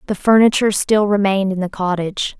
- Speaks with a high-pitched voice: Yes, high, 200 Hz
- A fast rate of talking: No, average, 175 wpm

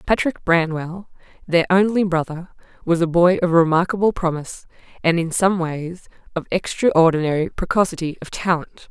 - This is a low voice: No, medium, 175 Hz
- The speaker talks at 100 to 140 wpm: Yes, slow, 135 wpm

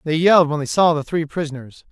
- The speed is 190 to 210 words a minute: No, fast, 250 wpm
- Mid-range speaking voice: Yes, medium, 160 Hz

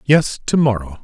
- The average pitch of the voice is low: Yes, low, 120 Hz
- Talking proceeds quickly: No, average, 175 wpm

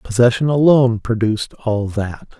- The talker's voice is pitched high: No, low, 115 Hz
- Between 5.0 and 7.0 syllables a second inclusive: No, 4.8 syllables/s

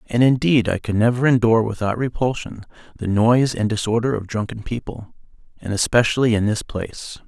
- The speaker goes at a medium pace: Yes, average, 165 wpm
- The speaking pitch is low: Yes, low, 115 Hz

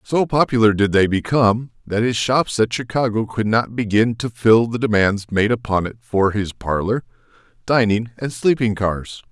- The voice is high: No, low, 110 Hz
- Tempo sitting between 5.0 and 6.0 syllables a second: No, 4.7 syllables/s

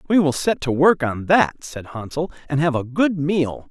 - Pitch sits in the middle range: Yes, medium, 150 Hz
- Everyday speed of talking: No, fast, 225 wpm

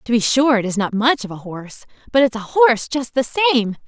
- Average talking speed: No, fast, 265 wpm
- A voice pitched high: Yes, high, 240 Hz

